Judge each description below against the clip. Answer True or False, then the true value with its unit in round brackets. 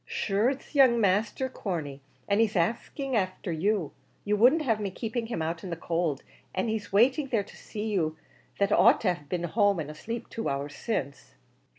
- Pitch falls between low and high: False (205 Hz)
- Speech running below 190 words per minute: False (205 wpm)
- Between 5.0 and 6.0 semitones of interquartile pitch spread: True (5.3 semitones)